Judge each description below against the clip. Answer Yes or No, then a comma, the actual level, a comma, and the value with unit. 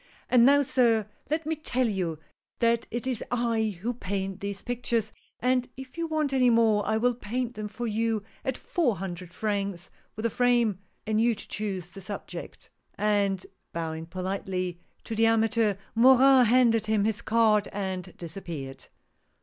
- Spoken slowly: No, average, 165 wpm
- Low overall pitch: No, high, 220 Hz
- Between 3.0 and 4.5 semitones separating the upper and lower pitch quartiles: Yes, average, 3.8 semitones